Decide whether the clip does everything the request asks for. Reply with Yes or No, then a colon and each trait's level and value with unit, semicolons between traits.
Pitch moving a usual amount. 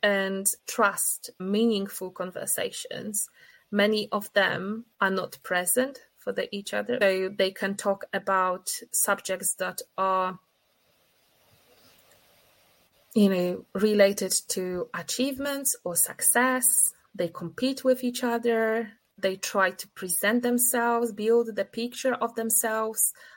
Yes: average, 3.8 semitones